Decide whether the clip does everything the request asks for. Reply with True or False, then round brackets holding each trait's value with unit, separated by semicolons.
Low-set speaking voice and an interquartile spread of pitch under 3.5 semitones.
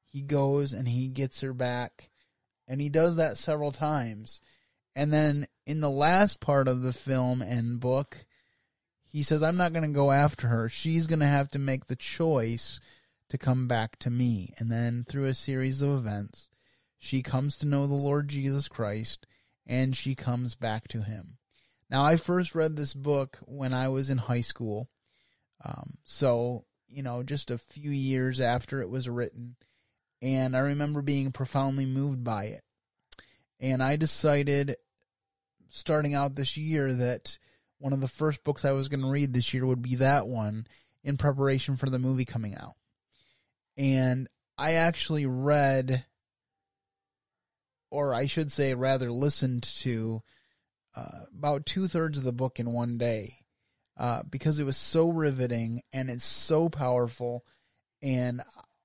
True (130 Hz; 2.7 semitones)